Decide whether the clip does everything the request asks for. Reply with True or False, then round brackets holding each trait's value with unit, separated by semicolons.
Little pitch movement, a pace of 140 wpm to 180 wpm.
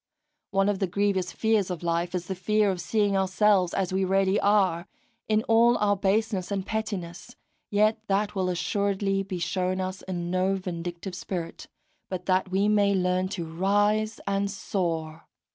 True (2.1 semitones; 165 wpm)